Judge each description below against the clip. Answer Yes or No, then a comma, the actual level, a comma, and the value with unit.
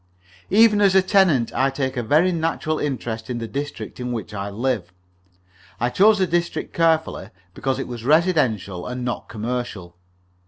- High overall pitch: No, low, 130 Hz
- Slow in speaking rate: No, average, 165 wpm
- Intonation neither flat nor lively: No, wide, 6.3 semitones